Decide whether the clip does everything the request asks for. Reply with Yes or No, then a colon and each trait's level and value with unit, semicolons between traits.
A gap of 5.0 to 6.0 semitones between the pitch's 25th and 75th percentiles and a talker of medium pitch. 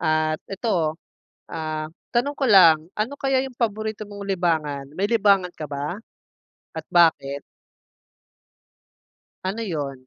Yes: wide, 5.4 semitones; medium, 180 Hz